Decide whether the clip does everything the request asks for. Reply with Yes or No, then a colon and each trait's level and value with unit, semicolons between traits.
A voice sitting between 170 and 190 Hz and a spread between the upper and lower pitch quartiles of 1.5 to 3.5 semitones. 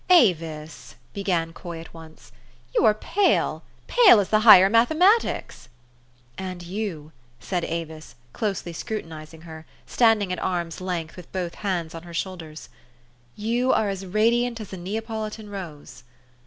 No: medium, 185 Hz; average, 4.8 semitones